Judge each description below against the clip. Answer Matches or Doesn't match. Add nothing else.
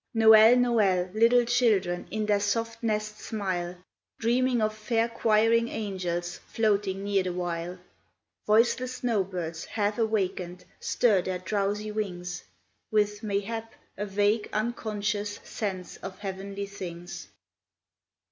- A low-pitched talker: Doesn't match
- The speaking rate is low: Matches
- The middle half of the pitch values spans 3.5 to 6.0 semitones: Doesn't match